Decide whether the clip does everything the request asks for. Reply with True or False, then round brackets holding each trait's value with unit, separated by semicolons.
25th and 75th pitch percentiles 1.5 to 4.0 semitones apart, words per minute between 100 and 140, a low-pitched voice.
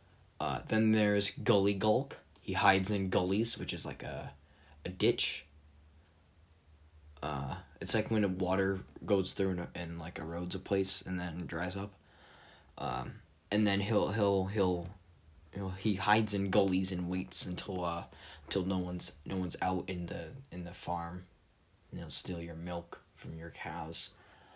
False (2.8 semitones; 165 wpm; 90 Hz)